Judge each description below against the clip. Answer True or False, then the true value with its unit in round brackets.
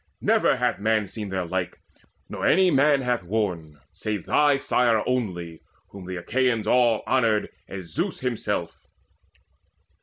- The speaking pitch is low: True (110 Hz)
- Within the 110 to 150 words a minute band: True (140 wpm)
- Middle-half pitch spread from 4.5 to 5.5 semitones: True (5.2 semitones)